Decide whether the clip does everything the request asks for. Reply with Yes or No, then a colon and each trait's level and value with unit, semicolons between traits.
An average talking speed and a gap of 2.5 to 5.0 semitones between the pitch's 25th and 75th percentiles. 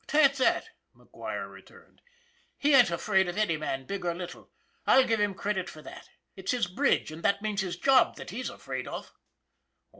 No: average, 185 wpm; wide, 5.4 semitones